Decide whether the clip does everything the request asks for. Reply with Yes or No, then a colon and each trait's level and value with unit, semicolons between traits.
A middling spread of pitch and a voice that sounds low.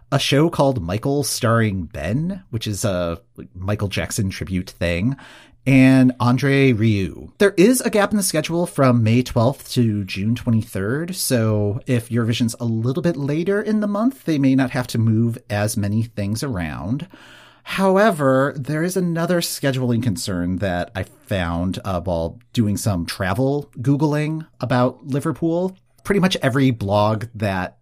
No: wide, 5.9 semitones; low, 125 Hz